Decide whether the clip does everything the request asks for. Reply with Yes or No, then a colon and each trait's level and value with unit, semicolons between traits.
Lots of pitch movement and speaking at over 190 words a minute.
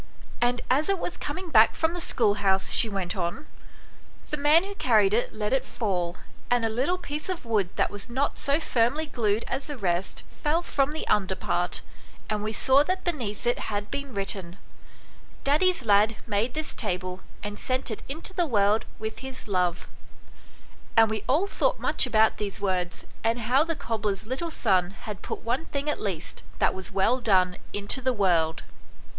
Yes: wide, 5.9 semitones; average, 200 wpm